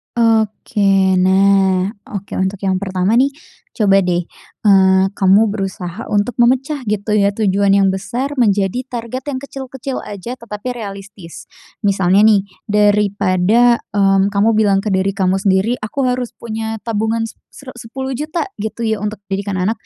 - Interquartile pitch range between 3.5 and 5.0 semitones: No, average, 3.1 semitones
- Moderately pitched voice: No, high, 205 Hz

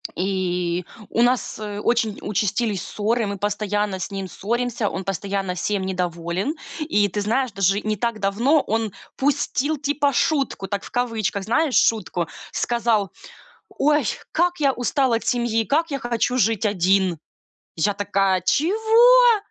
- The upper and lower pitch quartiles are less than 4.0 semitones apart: No, average, 4.7 semitones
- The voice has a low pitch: No, high, 215 Hz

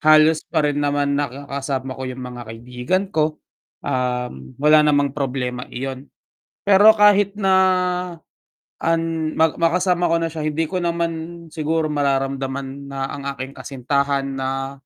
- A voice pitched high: No, medium, 145 Hz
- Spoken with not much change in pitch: No, average, 3.6 semitones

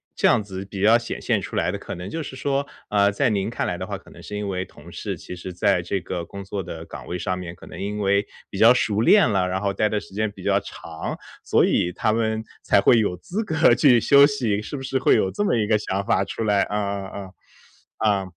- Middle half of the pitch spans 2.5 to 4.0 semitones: Yes, average, 3.2 semitones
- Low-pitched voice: Yes, low, 105 Hz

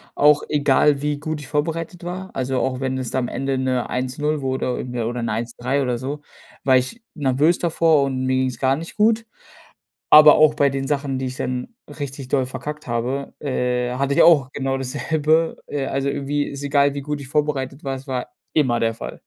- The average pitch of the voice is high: No, low, 135 Hz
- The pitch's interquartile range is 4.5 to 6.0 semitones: No, narrow, 2.4 semitones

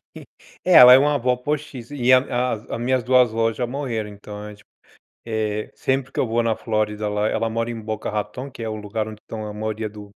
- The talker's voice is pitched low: Yes, low, 115 Hz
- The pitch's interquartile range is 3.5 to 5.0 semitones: No, average, 2.9 semitones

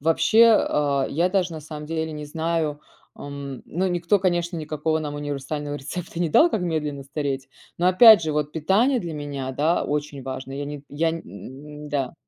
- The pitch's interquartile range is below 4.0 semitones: Yes, average, 2.8 semitones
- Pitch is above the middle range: No, medium, 150 Hz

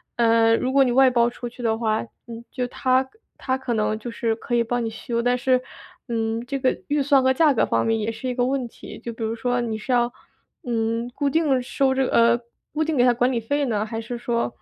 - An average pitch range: No, narrow, 2.3 semitones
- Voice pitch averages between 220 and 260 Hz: Yes, high, 240 Hz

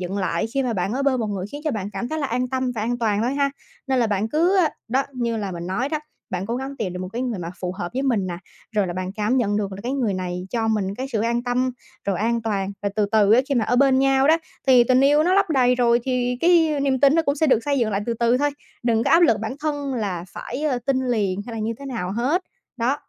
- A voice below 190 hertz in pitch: No, high, 240 Hz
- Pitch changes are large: No, average, 4.7 semitones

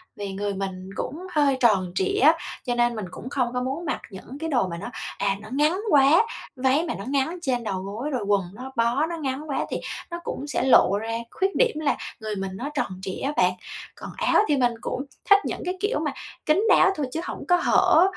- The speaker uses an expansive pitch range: Yes, wide, 6.9 semitones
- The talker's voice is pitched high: Yes, very high, 260 Hz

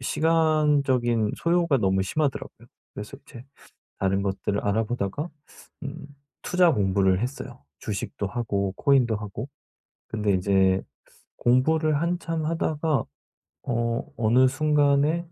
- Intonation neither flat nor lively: No, wide, 7.0 semitones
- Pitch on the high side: No, low, 125 Hz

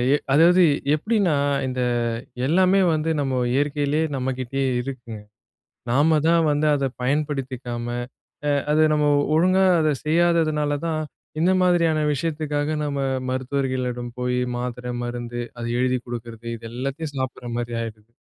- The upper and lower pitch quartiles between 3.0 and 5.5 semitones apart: Yes, average, 3.9 semitones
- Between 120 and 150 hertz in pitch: Yes, medium, 140 Hz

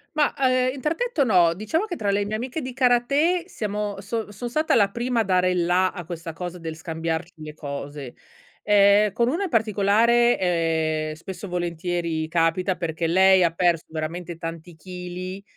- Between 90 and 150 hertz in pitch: No, medium, 185 Hz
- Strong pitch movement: Yes, wide, 5.9 semitones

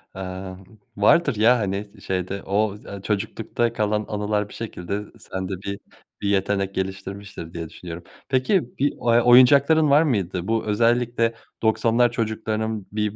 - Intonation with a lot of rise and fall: No, average, 3.1 semitones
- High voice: No, low, 105 Hz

